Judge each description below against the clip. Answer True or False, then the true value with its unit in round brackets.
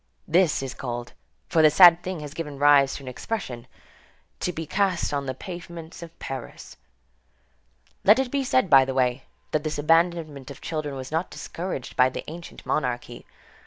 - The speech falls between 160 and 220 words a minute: True (175 wpm)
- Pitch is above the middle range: False (155 Hz)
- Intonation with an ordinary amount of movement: True (4.4 semitones)